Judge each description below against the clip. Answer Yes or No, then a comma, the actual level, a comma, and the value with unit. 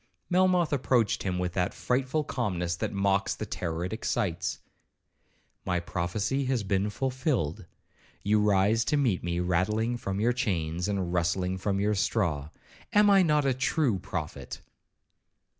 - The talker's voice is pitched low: Yes, low, 100 Hz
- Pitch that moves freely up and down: Yes, wide, 6.0 semitones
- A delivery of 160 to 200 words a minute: No, average, 140 wpm